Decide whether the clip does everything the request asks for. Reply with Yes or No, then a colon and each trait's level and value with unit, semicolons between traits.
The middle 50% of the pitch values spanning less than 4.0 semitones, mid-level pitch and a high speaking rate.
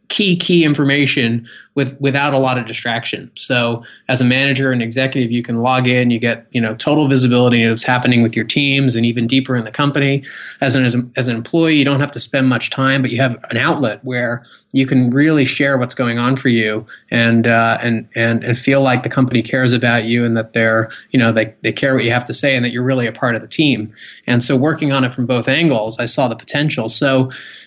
No: narrow, 2.5 semitones; low, 125 Hz; fast, 240 wpm